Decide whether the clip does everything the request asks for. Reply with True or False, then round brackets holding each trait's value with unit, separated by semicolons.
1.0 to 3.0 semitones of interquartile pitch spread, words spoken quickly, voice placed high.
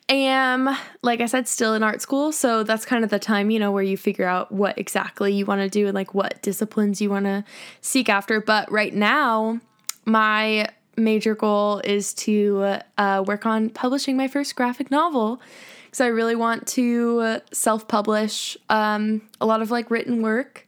False (2.6 semitones; 190 wpm; 220 Hz)